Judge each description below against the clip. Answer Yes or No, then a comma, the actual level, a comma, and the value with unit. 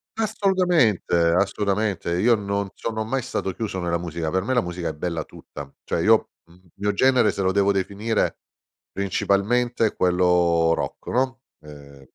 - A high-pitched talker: No, low, 100 Hz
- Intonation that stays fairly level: No, average, 4.7 semitones